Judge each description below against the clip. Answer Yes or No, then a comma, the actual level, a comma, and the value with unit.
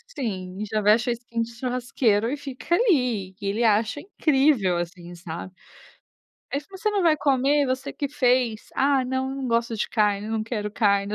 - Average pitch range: Yes, average, 4.5 semitones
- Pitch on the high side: Yes, high, 235 Hz